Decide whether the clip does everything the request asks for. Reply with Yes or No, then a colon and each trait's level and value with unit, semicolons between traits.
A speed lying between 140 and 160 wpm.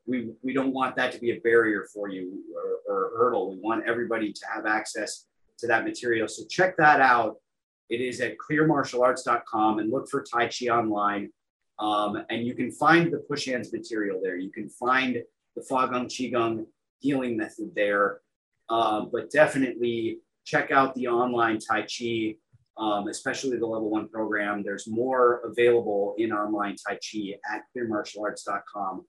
No: average, 170 wpm